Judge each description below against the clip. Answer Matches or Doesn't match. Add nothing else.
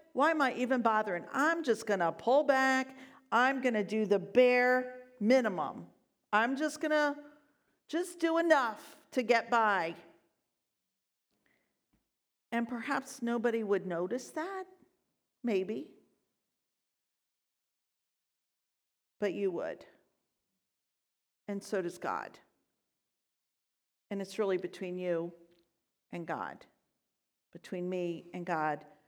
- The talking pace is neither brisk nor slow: Doesn't match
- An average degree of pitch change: Doesn't match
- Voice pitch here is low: Doesn't match